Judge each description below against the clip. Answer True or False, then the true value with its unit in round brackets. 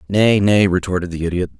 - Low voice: True (95 Hz)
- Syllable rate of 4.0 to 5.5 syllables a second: False (5.8 syllables/s)